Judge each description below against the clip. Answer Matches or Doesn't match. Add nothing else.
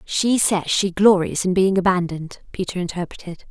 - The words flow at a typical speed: Matches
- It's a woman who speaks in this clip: Matches